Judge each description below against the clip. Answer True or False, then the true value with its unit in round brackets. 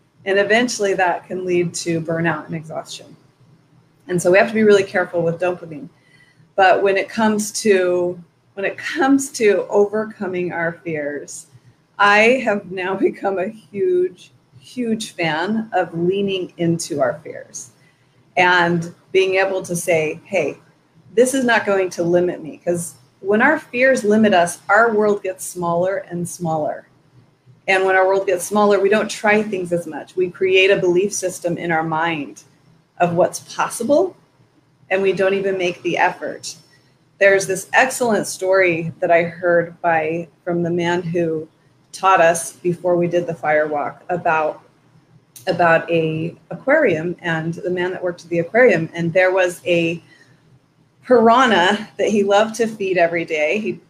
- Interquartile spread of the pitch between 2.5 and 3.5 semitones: True (3.1 semitones)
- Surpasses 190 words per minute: False (160 wpm)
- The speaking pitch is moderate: True (175 Hz)